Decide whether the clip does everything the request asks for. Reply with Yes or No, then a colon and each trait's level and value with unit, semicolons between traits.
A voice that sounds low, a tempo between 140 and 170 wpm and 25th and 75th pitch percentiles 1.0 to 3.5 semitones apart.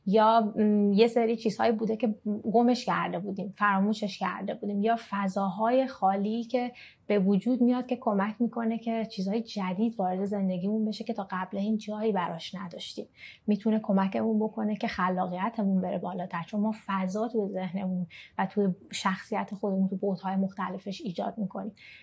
No: high, 205 Hz; fast, 155 wpm; narrow, 2.6 semitones